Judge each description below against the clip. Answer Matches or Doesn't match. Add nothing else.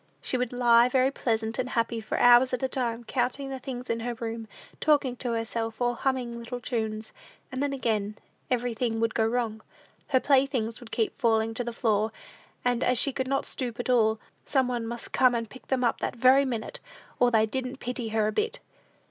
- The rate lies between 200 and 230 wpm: Matches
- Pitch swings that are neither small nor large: Doesn't match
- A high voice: Matches